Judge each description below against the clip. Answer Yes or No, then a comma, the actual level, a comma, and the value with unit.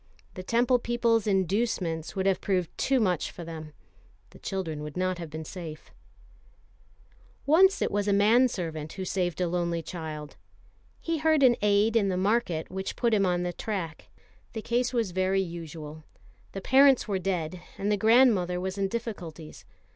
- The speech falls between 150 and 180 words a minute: Yes, average, 170 wpm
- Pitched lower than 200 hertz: Yes, high, 190 Hz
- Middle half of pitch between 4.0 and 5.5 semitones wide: Yes, average, 4.9 semitones